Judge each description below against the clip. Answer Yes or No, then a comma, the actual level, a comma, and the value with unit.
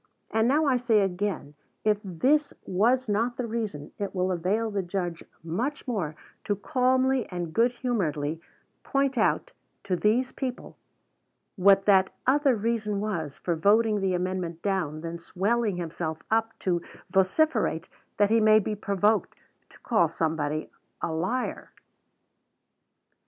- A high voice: Yes, high, 205 Hz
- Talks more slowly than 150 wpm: Yes, average, 140 wpm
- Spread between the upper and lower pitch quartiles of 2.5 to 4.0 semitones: No, average, 4.9 semitones